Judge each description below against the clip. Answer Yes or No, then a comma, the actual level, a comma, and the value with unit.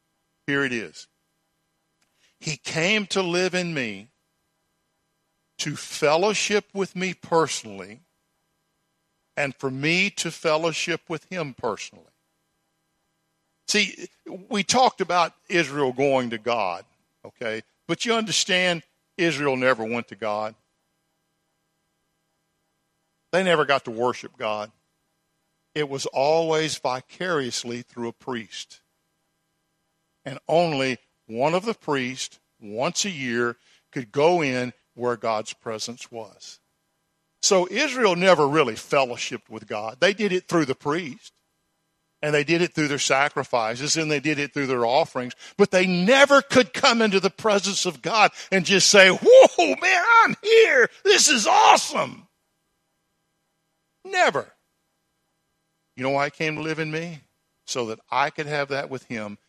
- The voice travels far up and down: No, average, 4.0 semitones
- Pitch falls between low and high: Yes, medium, 160 Hz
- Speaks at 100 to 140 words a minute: Yes, slow, 135 wpm